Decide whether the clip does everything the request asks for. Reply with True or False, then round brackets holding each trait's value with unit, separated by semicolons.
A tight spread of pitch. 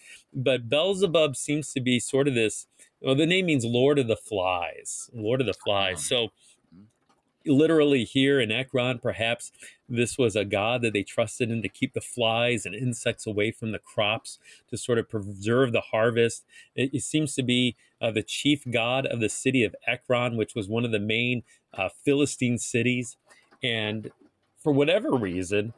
False (3.3 semitones)